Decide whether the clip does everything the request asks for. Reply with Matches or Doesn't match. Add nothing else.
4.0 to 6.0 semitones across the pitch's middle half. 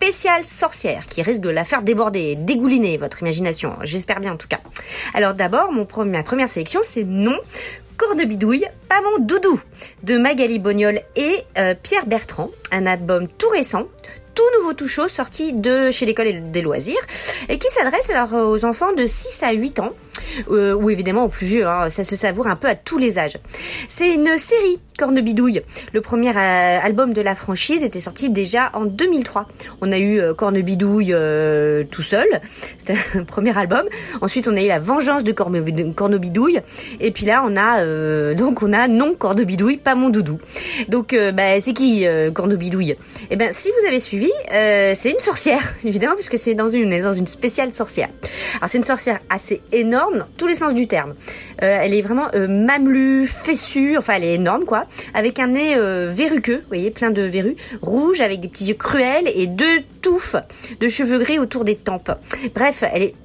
Matches